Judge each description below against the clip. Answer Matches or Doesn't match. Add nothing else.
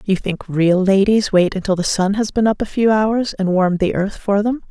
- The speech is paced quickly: Matches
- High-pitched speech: Matches